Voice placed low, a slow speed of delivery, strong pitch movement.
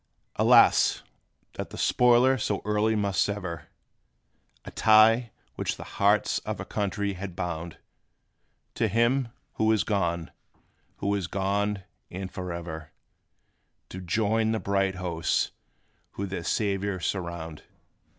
No: low, 100 Hz; slow, 120 wpm; average, 3.3 semitones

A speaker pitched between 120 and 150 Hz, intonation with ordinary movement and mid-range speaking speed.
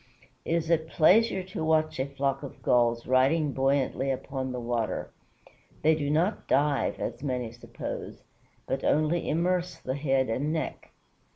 Yes: medium, 140 Hz; average, 3.5 semitones; average, 155 wpm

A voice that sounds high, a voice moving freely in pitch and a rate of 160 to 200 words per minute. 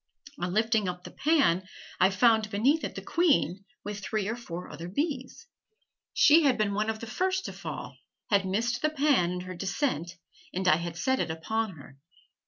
Yes: high, 215 Hz; wide, 6.4 semitones; average, 190 wpm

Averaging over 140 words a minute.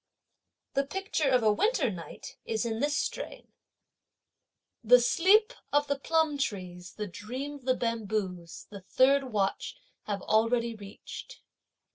No: slow, 135 wpm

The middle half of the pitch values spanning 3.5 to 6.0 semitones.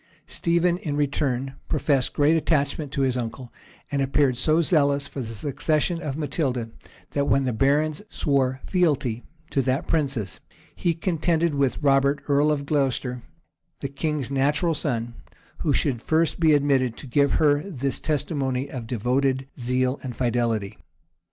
No: average, 2.8 semitones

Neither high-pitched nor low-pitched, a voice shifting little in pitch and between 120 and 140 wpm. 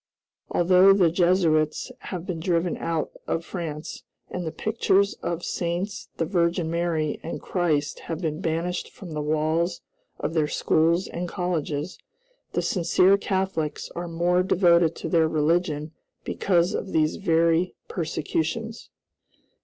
Yes: medium, 170 Hz; narrow, 2.2 semitones; slow, 135 wpm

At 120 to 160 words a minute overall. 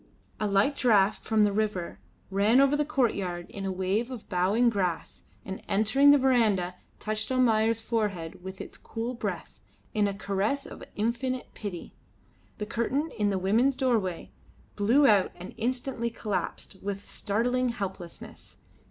Yes: average, 150 wpm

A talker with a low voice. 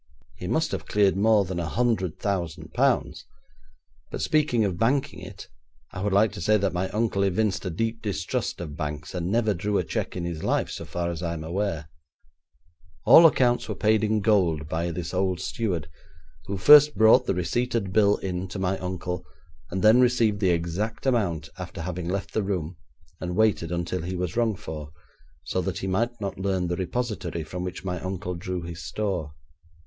Yes: very low, 95 Hz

